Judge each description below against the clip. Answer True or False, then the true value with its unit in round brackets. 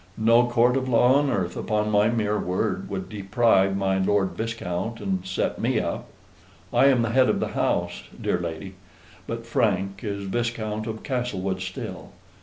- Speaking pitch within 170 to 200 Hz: False (105 Hz)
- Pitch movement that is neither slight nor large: True (3.4 semitones)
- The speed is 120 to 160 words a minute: False (170 wpm)